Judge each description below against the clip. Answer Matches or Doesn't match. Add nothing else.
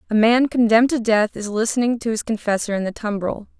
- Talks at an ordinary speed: Doesn't match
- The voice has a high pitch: Matches